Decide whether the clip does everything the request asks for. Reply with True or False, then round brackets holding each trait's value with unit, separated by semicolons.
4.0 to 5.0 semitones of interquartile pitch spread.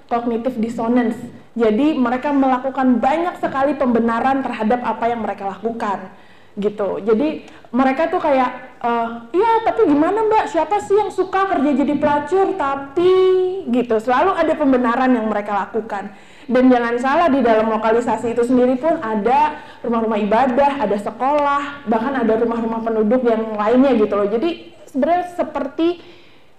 True (4.6 semitones)